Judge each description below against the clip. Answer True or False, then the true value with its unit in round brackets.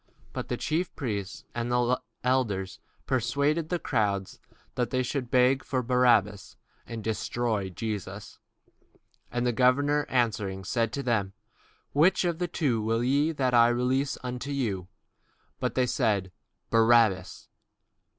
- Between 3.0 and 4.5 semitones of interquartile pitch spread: True (3.7 semitones)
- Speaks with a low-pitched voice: True (120 Hz)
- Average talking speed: False (125 wpm)